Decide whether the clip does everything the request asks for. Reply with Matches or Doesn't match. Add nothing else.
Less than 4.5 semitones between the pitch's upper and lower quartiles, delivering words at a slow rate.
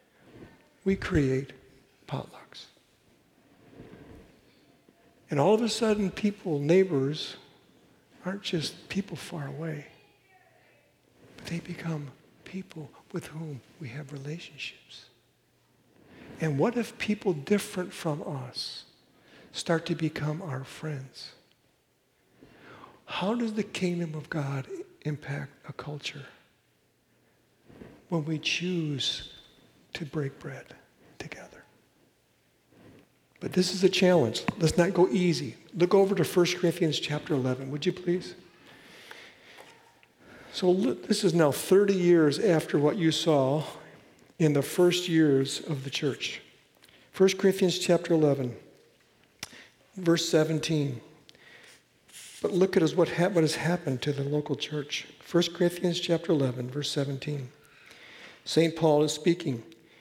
Matches